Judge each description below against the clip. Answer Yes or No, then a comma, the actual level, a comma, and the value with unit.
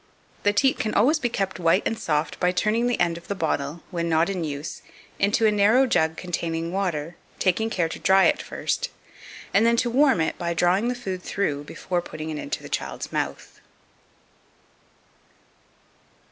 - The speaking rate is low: No, average, 180 wpm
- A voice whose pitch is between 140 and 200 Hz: Yes, medium, 185 Hz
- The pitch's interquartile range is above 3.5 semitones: Yes, average, 4.9 semitones